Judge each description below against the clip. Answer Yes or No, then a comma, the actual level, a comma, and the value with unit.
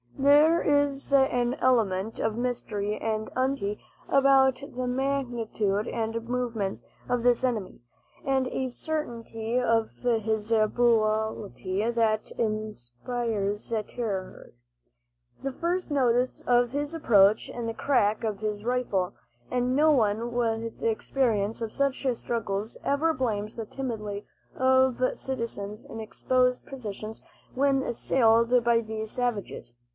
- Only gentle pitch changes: No, average, 3.1 semitones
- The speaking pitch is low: No, high, 235 Hz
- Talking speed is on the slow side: Yes, slow, 120 wpm